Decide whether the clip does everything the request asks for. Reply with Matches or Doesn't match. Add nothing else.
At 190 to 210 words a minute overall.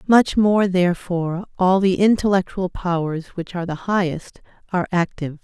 Doesn't match